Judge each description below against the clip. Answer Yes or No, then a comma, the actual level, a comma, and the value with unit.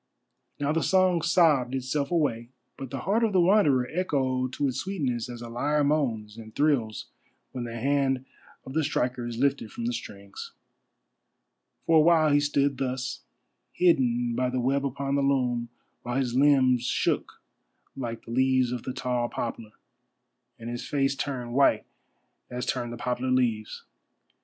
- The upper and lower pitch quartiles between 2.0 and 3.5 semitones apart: Yes, average, 2.9 semitones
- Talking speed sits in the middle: Yes, average, 165 wpm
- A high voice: No, low, 130 Hz